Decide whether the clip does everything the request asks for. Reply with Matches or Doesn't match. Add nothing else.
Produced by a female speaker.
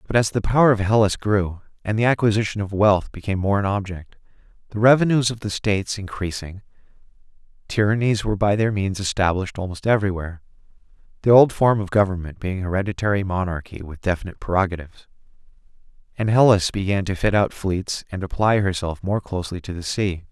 Doesn't match